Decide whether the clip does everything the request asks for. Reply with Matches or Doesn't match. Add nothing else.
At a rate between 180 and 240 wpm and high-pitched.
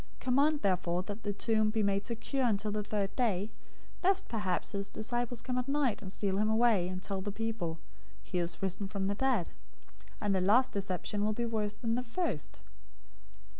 Matches